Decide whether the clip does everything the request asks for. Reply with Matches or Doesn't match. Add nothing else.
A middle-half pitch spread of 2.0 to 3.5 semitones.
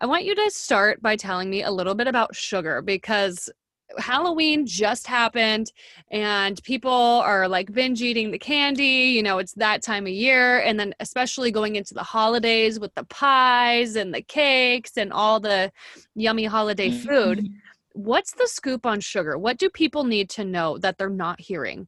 Doesn't match